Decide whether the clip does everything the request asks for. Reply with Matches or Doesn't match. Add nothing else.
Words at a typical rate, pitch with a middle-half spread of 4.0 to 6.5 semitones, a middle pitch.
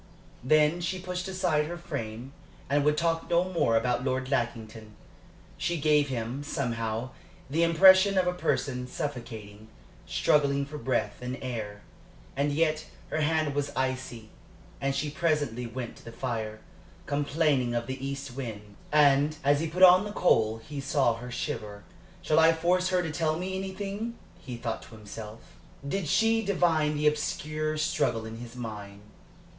Matches